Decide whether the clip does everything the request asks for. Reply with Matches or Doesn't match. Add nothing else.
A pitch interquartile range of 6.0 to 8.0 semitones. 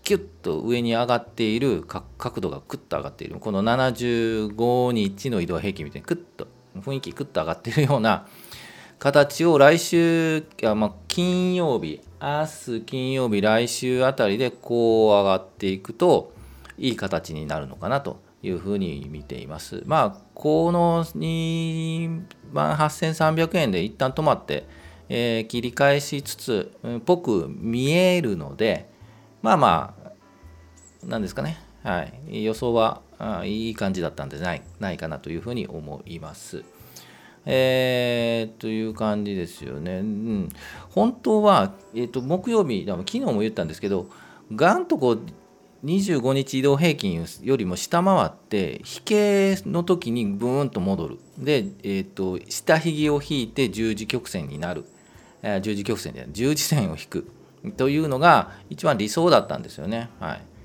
Matches